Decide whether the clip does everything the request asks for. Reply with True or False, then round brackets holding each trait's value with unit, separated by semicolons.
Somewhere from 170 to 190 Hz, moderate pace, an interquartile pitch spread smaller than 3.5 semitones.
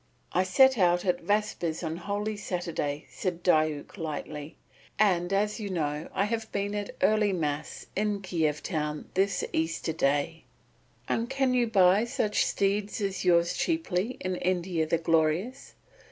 False (185 Hz; 150 wpm; 4.3 semitones)